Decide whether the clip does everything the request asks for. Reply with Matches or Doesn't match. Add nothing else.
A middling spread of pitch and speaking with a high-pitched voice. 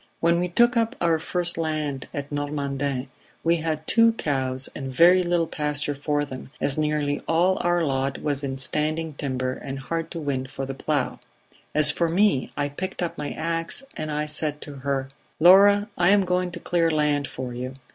Doesn't match